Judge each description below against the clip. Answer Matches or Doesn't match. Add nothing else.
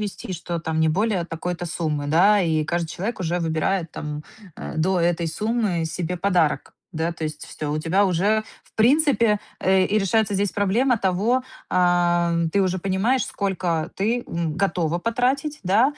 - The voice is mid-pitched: Matches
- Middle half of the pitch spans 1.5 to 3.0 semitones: Doesn't match